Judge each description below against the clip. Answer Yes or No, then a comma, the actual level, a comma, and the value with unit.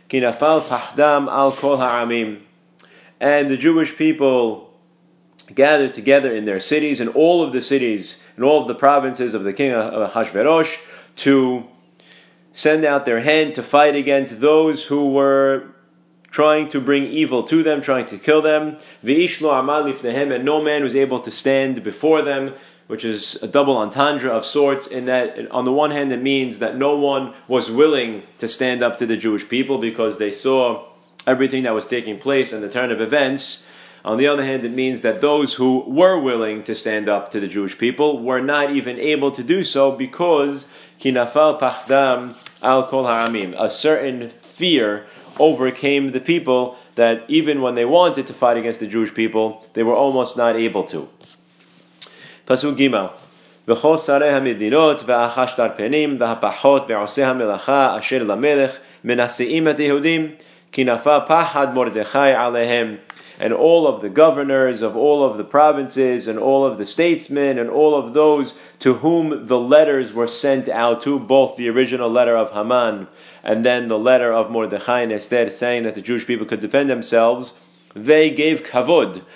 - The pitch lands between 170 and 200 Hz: No, low, 135 Hz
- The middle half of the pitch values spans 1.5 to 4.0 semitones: Yes, average, 3.5 semitones